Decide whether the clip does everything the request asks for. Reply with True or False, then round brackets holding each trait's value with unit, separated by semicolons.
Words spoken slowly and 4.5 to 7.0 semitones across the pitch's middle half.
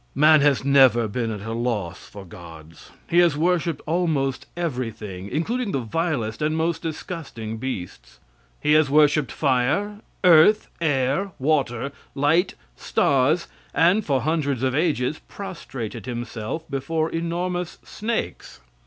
True (125 wpm; 5.5 semitones)